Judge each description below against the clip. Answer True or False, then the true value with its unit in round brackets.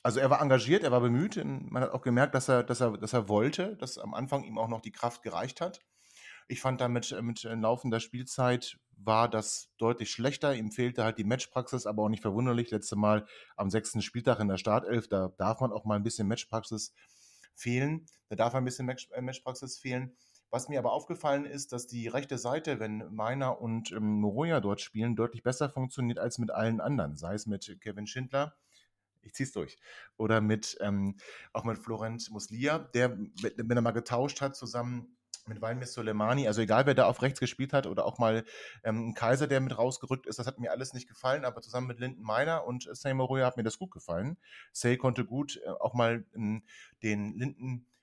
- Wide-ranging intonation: False (2.8 semitones)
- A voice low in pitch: True (120 Hz)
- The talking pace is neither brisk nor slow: False (200 wpm)